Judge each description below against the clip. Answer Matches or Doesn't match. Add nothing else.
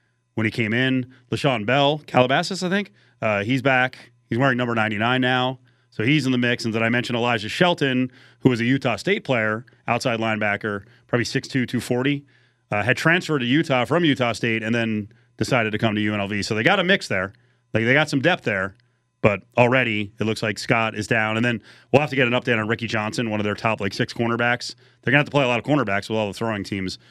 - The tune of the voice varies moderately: Matches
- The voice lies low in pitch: Matches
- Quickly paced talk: Matches